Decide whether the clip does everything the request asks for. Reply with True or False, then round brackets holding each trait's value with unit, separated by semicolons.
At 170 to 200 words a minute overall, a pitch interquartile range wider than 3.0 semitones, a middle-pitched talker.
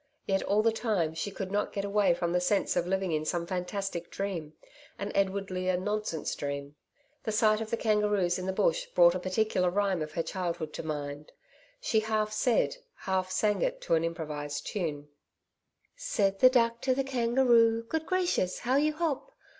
False (190 wpm; 4.7 semitones; 200 Hz)